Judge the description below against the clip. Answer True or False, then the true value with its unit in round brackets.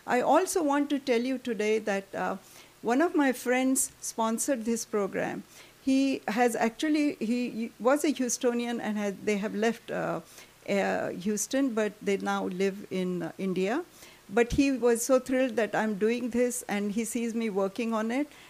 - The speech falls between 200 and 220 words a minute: False (175 wpm)